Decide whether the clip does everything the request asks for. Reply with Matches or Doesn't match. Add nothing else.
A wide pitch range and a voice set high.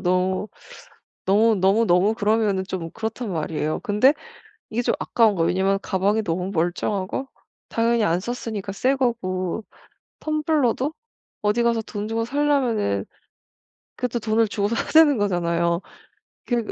Doesn't match